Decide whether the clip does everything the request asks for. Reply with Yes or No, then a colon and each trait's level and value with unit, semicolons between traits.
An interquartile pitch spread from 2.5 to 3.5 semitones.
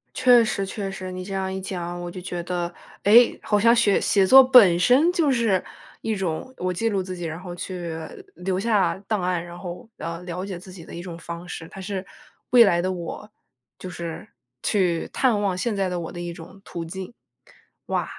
Yes: average, 2.9 semitones